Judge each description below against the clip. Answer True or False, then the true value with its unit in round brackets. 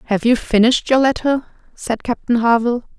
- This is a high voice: True (240 Hz)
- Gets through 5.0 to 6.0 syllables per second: True (5.9 syllables/s)